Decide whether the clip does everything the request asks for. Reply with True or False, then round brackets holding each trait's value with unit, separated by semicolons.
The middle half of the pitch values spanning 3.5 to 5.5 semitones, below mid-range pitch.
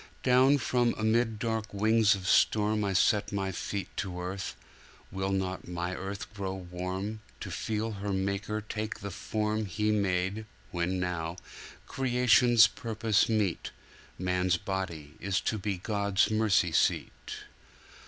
False (2.7 semitones; 100 Hz)